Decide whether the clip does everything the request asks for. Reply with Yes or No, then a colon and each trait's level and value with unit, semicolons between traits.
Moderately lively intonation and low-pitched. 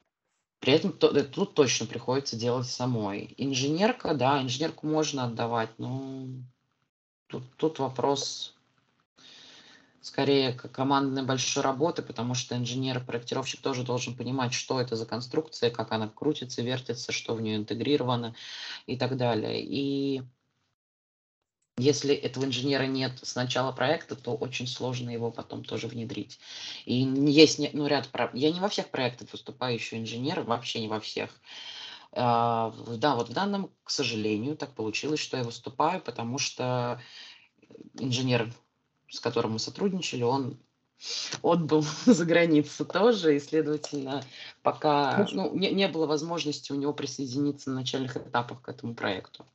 Yes: average, 3.6 semitones; low, 130 Hz